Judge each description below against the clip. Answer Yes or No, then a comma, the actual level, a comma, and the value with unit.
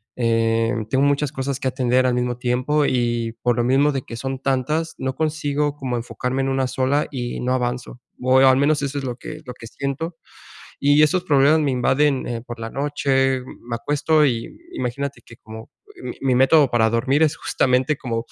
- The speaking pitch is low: Yes, low, 130 Hz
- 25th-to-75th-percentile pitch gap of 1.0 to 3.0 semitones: Yes, narrow, 2.6 semitones